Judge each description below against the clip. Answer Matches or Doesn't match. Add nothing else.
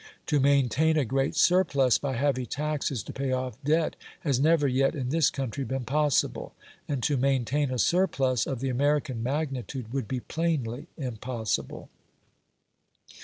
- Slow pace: Doesn't match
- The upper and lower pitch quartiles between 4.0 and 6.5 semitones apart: Doesn't match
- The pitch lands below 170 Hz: Matches